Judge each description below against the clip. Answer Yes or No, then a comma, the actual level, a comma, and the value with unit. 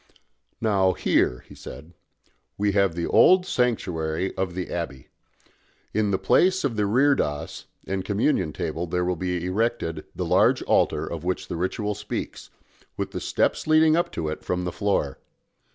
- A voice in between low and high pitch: No, very low, 95 Hz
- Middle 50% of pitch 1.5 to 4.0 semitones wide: No, average, 4.5 semitones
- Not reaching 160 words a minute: No, average, 165 wpm